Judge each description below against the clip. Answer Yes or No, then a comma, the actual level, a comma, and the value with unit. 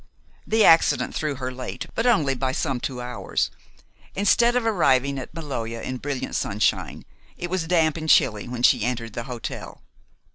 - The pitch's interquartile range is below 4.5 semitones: No, average, 4.9 semitones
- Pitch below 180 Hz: Yes, low, 135 Hz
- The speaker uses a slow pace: No, average, 170 wpm